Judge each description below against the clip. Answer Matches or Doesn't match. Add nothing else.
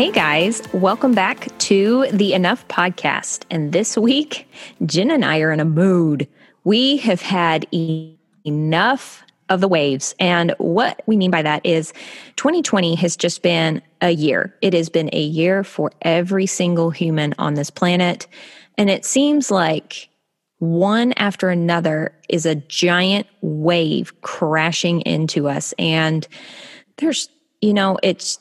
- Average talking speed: Matches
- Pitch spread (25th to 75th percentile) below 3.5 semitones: Doesn't match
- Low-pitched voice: Doesn't match